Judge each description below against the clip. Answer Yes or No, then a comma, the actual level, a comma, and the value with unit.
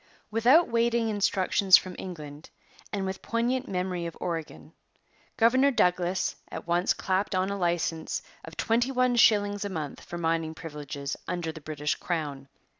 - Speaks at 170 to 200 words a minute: No, average, 150 wpm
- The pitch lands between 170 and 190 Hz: Yes, medium, 185 Hz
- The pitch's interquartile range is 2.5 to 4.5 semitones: No, average, 5.1 semitones